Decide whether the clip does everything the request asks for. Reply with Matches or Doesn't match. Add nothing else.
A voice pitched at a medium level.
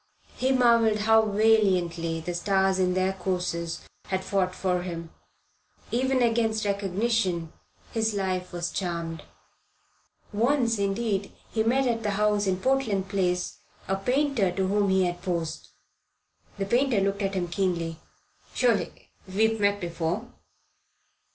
Doesn't match